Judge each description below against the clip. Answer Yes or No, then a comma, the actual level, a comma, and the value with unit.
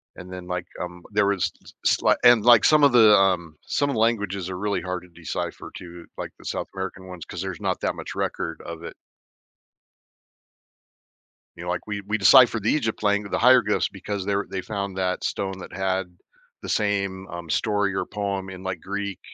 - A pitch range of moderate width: No, narrow, 2.3 semitones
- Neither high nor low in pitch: No, very low, 95 Hz